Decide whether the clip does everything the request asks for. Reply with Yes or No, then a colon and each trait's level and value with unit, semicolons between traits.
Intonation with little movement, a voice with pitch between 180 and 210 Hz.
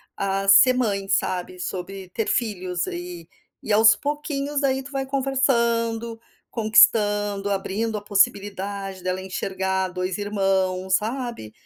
No: average, 3.6 semitones; high, 205 Hz